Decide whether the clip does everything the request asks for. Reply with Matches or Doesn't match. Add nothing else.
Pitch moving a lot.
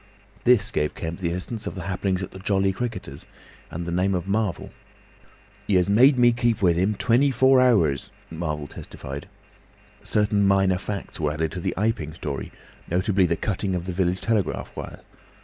Doesn't match